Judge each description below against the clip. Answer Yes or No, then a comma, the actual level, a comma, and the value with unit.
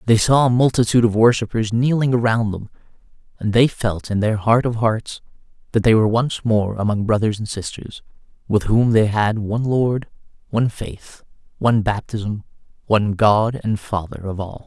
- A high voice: No, low, 110 Hz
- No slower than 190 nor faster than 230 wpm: No, average, 170 wpm